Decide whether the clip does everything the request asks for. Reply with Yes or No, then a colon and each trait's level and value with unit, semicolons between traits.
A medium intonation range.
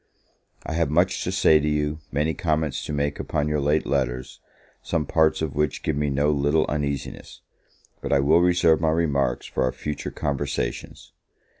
No: narrow, 1.8 semitones